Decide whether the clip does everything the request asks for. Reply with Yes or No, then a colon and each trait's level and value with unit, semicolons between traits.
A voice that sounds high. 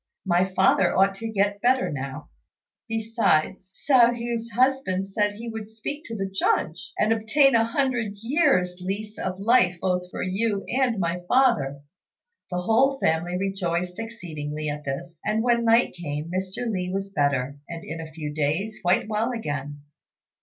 Yes: high, 195 Hz